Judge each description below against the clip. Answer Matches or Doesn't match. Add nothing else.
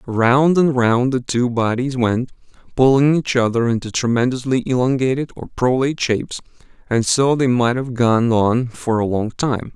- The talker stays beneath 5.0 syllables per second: Matches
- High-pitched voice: Doesn't match